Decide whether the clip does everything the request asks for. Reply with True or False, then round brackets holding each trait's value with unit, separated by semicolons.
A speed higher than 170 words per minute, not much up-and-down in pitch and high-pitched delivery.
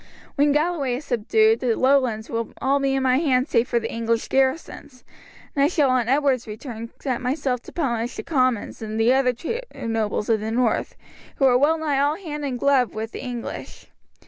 False (200 wpm; 3.4 semitones; 255 Hz)